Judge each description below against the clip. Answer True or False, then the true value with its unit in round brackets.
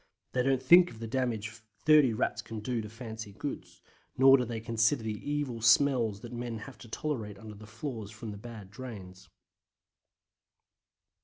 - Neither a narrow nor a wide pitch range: True (3.2 semitones)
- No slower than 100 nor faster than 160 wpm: False (175 wpm)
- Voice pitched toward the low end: True (115 Hz)